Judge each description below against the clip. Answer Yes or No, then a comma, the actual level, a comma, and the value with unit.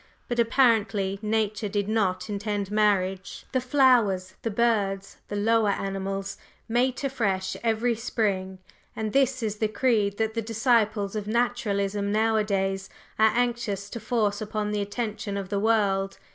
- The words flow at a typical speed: Yes, average, 145 wpm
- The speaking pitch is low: No, high, 210 Hz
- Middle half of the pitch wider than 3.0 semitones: No, narrow, 2.4 semitones